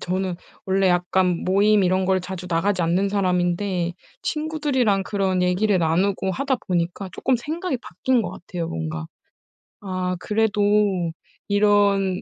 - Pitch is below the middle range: No, high, 190 Hz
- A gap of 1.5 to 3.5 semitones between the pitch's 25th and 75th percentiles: Yes, narrow, 2.4 semitones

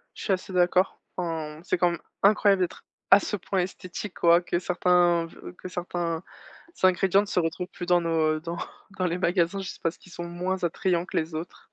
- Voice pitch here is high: No, medium, 175 Hz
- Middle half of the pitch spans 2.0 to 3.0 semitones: No, narrow, 1.6 semitones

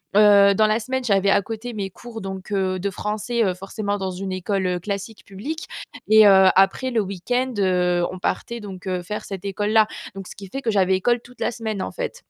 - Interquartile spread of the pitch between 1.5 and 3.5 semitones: Yes, average, 2.8 semitones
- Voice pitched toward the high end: Yes, high, 200 Hz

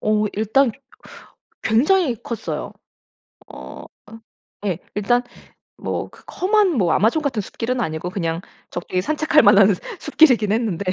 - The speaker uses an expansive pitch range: Yes, wide, 5.9 semitones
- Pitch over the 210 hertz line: Yes, high, 220 Hz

